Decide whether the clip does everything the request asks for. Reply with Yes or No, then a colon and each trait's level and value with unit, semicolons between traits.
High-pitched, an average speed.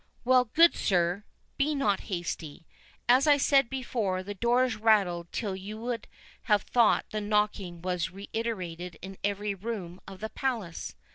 Yes: high, 210 Hz; average, 150 wpm